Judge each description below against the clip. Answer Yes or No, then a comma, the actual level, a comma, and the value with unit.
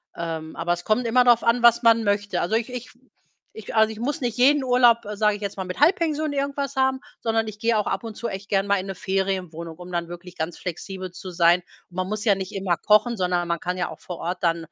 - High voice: Yes, high, 205 Hz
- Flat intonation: No, average, 4.7 semitones